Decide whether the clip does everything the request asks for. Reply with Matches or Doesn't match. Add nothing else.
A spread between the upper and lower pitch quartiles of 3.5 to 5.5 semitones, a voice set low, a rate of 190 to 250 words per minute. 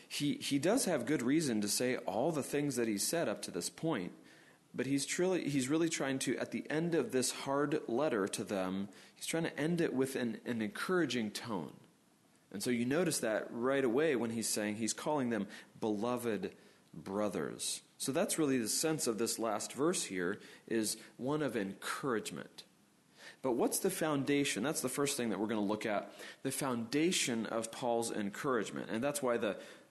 Matches